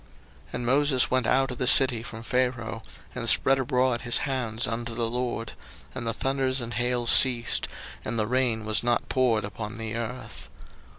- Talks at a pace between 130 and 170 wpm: No, average, 180 wpm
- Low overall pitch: Yes, low, 120 Hz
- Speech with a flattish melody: Yes, narrow, 2.1 semitones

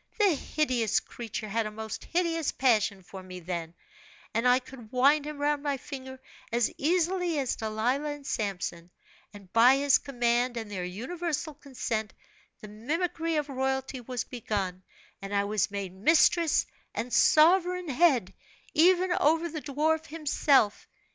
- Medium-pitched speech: No, very high, 260 Hz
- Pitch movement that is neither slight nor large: No, wide, 6.1 semitones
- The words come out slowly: No, average, 150 wpm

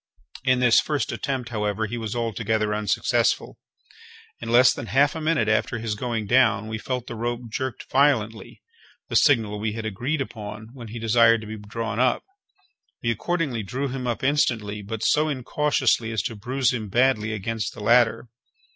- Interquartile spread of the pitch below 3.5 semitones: Yes, average, 2.9 semitones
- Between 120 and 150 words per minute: No, average, 175 wpm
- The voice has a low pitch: Yes, low, 115 Hz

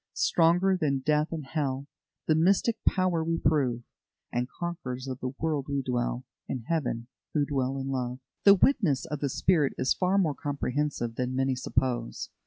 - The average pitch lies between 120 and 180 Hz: Yes, medium, 140 Hz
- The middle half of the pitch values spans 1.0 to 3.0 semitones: No, average, 4.2 semitones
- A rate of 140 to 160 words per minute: No, average, 170 wpm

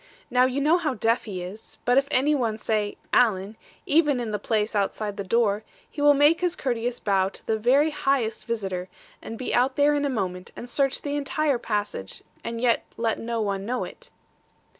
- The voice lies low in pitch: No, high, 235 Hz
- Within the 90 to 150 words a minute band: No, fast, 205 wpm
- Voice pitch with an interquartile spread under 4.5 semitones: No, average, 4.9 semitones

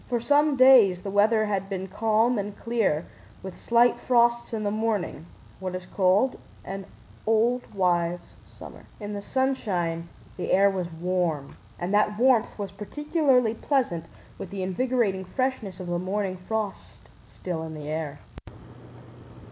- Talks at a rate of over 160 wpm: No, average, 145 wpm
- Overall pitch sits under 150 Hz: No, high, 205 Hz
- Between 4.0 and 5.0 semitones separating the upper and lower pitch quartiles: Yes, average, 4.3 semitones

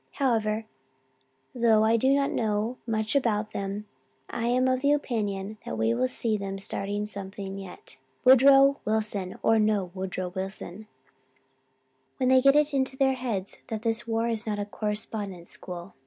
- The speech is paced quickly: No, average, 160 wpm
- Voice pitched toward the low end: No, high, 215 Hz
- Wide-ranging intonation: No, average, 3.9 semitones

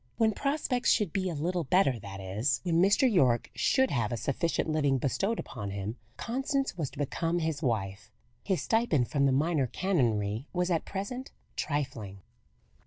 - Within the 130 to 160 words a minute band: No, average, 170 wpm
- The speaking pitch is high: No, medium, 155 Hz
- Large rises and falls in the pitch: Yes, wide, 8.3 semitones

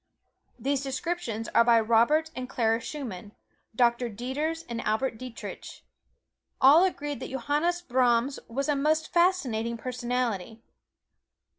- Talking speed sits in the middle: No, slow, 120 wpm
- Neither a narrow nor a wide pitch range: Yes, average, 4.1 semitones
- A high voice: Yes, very high, 255 Hz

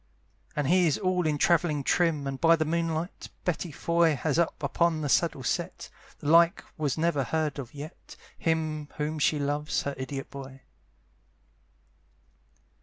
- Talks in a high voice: No, medium, 155 Hz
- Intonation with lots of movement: No, average, 2.7 semitones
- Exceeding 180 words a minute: No, average, 155 wpm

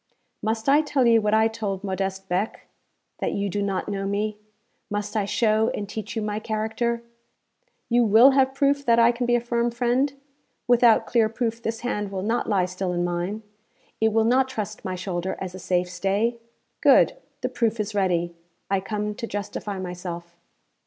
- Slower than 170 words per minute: No, average, 185 wpm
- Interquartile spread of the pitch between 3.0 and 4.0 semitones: Yes, average, 3.3 semitones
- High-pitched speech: Yes, high, 215 Hz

